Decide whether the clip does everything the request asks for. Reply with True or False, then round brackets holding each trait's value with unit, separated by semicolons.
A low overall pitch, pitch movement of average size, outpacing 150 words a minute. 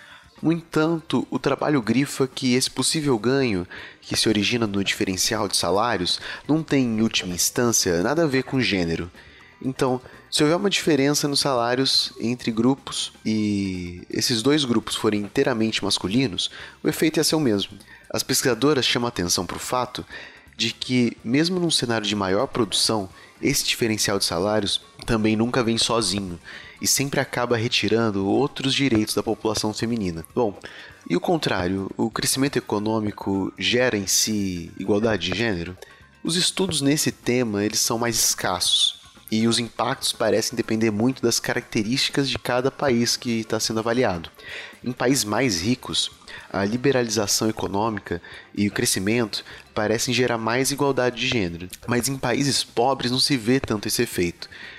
True (115 Hz; 4.1 semitones; 160 wpm)